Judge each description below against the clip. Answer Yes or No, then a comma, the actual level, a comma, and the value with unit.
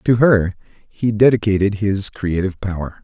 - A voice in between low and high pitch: No, low, 105 Hz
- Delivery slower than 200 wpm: Yes, average, 140 wpm